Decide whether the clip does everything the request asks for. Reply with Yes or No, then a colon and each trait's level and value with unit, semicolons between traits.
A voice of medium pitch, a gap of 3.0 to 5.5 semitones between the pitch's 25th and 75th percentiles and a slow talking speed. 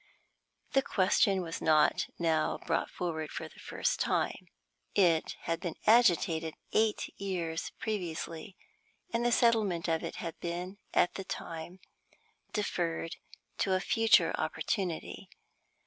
Yes: medium, 180 Hz; average, 3.6 semitones; slow, 125 wpm